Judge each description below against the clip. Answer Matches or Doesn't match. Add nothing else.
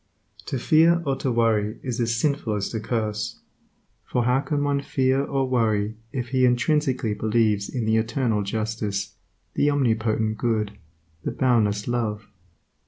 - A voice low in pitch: Matches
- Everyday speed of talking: Matches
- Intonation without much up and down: Doesn't match